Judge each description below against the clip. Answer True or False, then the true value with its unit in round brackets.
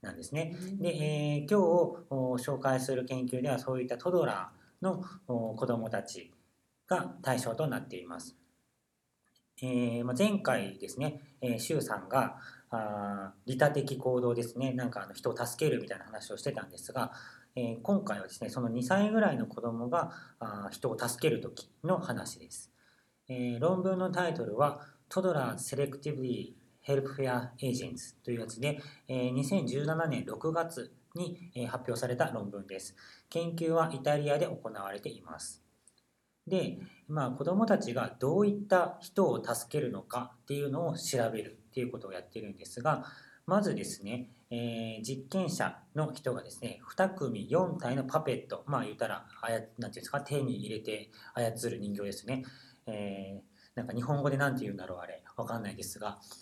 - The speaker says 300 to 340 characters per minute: True (320 characters per minute)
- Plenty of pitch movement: False (4.9 semitones)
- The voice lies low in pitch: True (130 Hz)